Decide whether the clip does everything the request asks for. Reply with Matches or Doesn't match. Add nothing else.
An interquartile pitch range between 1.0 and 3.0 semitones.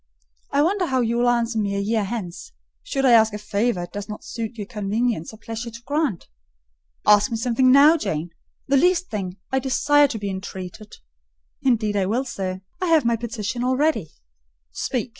Doesn't match